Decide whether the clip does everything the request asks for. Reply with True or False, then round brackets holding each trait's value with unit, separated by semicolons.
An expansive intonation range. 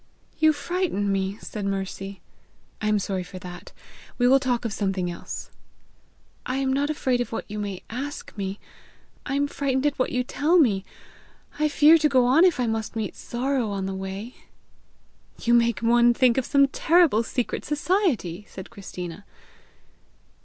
True (5.9 semitones)